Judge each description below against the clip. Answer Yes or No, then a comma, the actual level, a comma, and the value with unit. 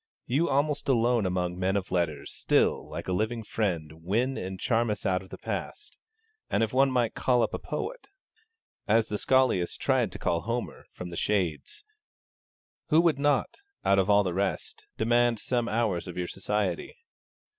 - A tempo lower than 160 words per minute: No, average, 175 wpm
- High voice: No, low, 110 Hz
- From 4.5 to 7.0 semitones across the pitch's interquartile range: Yes, average, 5.2 semitones